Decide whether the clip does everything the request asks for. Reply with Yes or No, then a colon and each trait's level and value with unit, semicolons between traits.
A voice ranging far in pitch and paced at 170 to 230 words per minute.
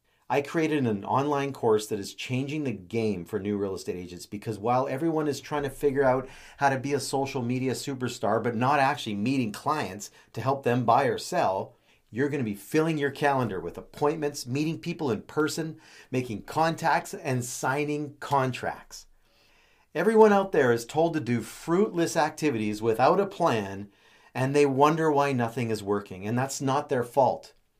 No: average, 4.3 semitones; average, 180 wpm